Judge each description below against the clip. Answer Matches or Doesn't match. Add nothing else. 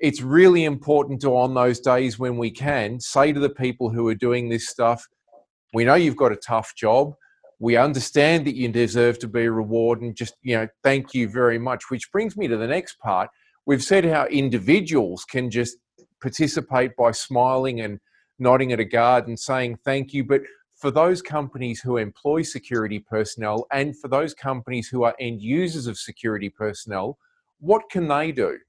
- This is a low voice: Matches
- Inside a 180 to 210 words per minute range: Matches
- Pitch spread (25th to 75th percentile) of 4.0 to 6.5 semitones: Doesn't match